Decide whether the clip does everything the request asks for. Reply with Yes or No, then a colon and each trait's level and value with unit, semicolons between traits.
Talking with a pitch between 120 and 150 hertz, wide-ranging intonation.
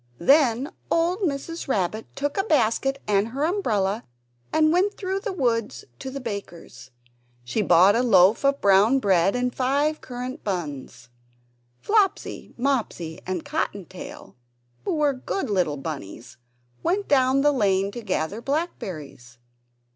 No: high, 235 Hz; wide, 7.2 semitones